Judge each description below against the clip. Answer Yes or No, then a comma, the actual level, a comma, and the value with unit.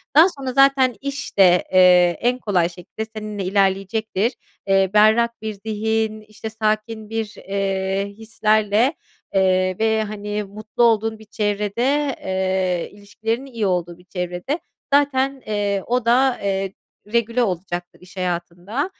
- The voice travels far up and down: No, average, 3.3 semitones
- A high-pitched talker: Yes, high, 215 Hz